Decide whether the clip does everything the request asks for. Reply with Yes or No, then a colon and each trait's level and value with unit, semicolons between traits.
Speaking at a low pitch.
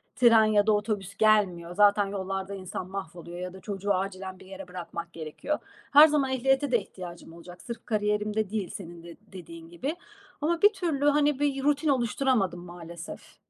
No: high, 200 Hz